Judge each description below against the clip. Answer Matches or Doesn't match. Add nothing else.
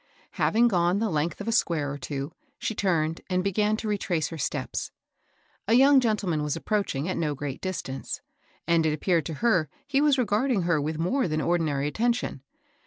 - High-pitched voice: Doesn't match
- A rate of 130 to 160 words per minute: Doesn't match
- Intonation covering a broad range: Matches